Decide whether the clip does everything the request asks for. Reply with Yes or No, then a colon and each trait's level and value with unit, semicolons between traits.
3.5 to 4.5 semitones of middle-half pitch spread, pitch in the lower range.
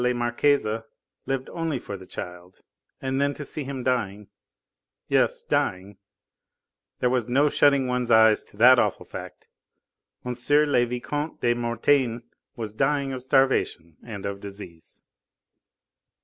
Yes: average, 4.0 semitones; low, 125 Hz